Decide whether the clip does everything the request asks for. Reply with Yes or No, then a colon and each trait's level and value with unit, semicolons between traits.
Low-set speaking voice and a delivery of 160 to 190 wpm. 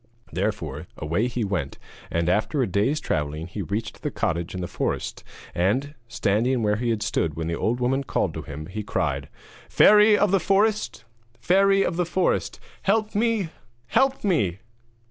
Yes: low, 115 Hz; average, 170 wpm